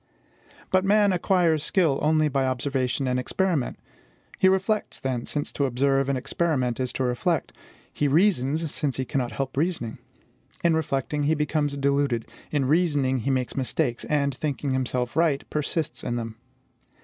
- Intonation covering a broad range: No, average, 3.6 semitones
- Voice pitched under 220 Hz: Yes, medium, 140 Hz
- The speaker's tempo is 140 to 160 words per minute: Yes, average, 155 wpm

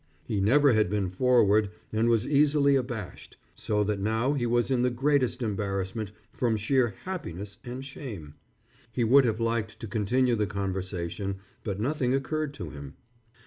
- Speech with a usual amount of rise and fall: Yes, average, 4.3 semitones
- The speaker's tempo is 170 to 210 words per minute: No, average, 160 wpm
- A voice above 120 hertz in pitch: No, low, 115 Hz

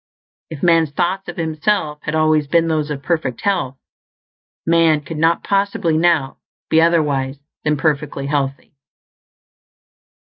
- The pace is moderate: No, slow, 130 wpm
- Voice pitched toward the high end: No, medium, 155 Hz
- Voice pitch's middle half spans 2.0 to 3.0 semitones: Yes, narrow, 2.5 semitones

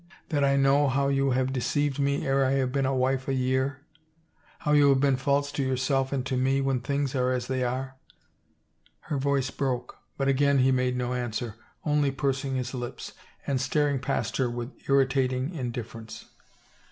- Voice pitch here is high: No, low, 135 Hz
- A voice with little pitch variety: Yes, narrow, 1.5 semitones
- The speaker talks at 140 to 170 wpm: No, average, 190 wpm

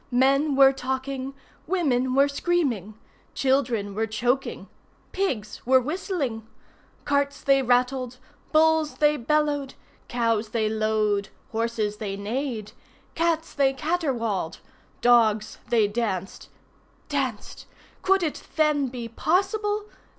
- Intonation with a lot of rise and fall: No, average, 4.9 semitones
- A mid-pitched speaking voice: No, very high, 260 Hz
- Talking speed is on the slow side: Yes, slow, 105 wpm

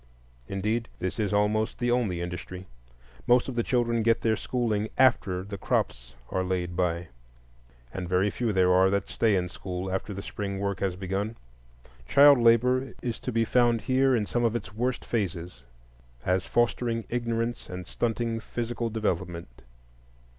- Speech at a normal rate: Yes, average, 160 wpm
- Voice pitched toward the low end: Yes, low, 105 Hz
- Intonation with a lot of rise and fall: No, average, 4.2 semitones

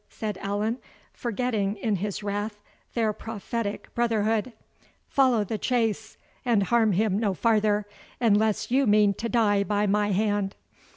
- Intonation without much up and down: Yes, narrow, 2.0 semitones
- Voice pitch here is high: Yes, high, 215 Hz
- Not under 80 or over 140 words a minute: Yes, slow, 135 wpm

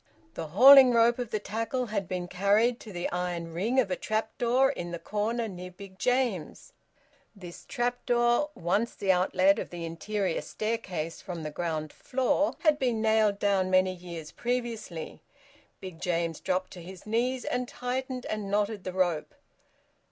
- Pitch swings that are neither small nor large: Yes, average, 5.0 semitones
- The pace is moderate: Yes, average, 165 wpm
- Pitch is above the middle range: Yes, high, 200 Hz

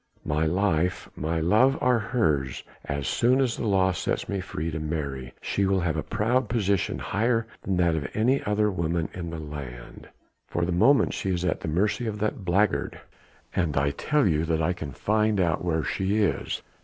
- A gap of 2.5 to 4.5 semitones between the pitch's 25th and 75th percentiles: No, average, 5.1 semitones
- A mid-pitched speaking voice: No, very low, 90 Hz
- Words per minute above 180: Yes, average, 200 wpm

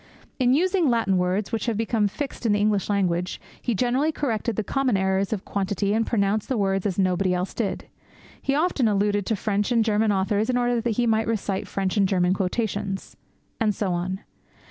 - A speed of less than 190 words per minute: No, average, 195 wpm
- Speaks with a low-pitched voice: No, high, 210 Hz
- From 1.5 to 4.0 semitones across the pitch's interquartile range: Yes, average, 3.2 semitones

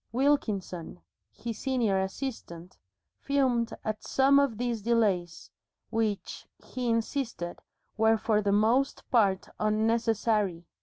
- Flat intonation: No, average, 3.4 semitones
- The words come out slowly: Yes, slow, 105 wpm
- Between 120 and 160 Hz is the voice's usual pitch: No, high, 225 Hz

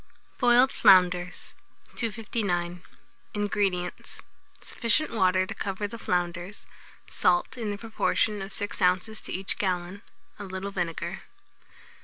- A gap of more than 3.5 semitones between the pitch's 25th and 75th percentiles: No, average, 2.9 semitones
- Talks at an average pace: No, slow, 115 wpm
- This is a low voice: No, high, 195 Hz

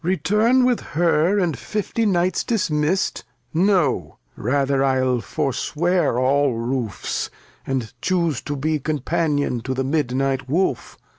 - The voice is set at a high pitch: No, medium, 150 Hz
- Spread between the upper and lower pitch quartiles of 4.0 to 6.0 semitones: Yes, average, 5.3 semitones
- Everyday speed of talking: No, slow, 125 wpm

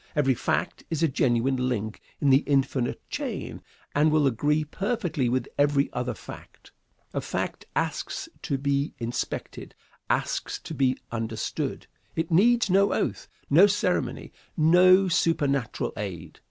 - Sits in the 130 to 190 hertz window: Yes, medium, 140 Hz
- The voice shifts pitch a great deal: No, average, 4.8 semitones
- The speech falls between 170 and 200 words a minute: No, slow, 135 wpm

